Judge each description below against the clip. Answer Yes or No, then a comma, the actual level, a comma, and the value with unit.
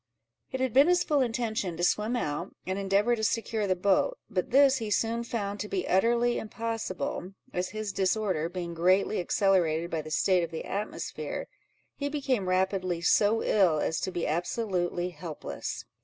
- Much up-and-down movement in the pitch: No, average, 4.3 semitones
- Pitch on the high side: Yes, high, 195 Hz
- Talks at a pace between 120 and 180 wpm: Yes, average, 170 wpm